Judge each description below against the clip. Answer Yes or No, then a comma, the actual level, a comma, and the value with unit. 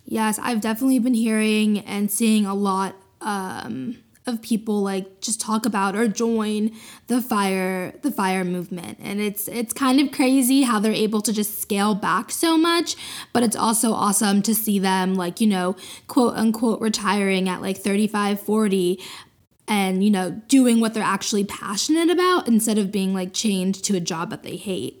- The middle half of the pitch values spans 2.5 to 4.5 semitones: Yes, average, 3.2 semitones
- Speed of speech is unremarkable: Yes, average, 180 wpm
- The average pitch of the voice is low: No, high, 215 Hz